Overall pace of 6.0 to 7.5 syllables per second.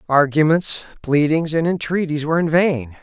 No: 4.9 syllables/s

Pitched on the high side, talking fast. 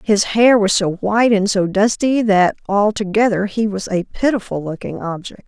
No: high, 205 Hz; average, 175 wpm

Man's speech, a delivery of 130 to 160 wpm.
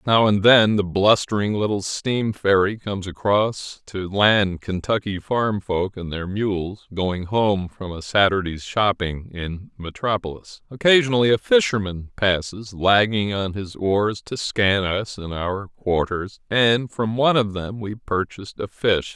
Yes: male; average, 155 wpm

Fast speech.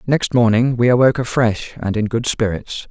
No: average, 185 wpm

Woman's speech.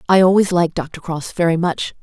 Yes: female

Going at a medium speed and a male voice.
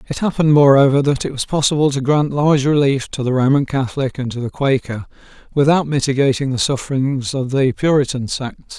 Yes: average, 185 wpm; male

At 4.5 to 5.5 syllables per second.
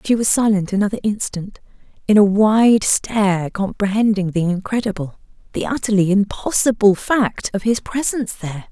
Yes: 5.1 syllables/s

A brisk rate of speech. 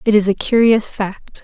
Yes: fast, 210 wpm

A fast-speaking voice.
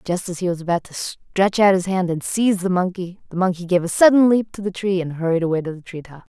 Yes: fast, 285 wpm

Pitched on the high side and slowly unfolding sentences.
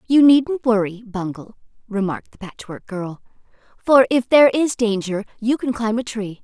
No: high, 225 Hz; average, 170 wpm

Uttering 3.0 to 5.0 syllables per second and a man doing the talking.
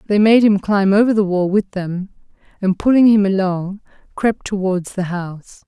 No: 4.7 syllables/s; female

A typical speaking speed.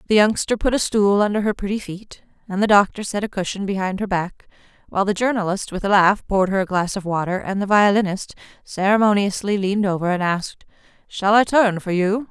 No: fast, 210 wpm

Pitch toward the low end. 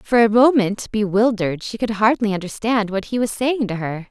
No: high, 215 Hz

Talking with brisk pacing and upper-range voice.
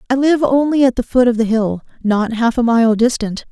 Yes: fast, 240 wpm; high, 240 Hz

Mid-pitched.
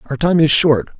Yes: medium, 150 Hz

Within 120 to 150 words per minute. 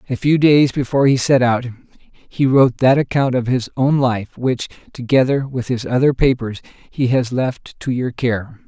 No: average, 185 wpm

